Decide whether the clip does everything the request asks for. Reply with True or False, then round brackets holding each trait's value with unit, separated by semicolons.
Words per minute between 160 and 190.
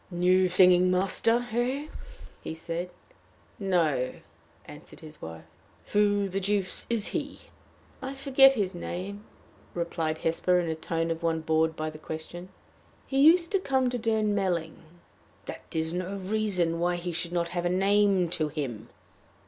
False (150 wpm)